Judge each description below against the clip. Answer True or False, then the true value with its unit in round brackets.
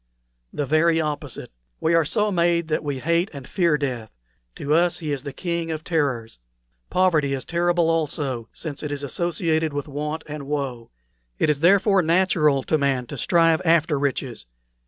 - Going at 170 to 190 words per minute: True (175 wpm)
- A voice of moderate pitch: True (155 Hz)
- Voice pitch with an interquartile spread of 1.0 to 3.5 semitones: True (3.1 semitones)